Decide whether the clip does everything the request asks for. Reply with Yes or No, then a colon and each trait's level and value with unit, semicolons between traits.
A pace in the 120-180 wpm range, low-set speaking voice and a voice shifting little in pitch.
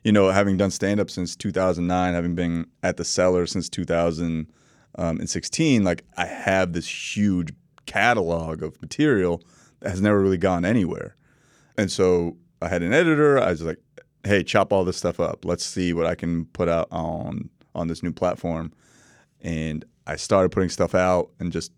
Yes: average, 175 wpm; very low, 90 Hz; narrow, 2.1 semitones